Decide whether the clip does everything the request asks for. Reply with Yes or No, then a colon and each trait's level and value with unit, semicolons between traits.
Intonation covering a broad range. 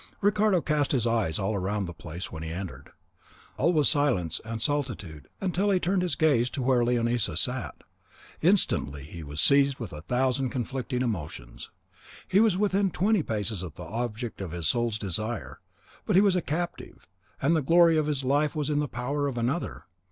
Yes: wide, 7.6 semitones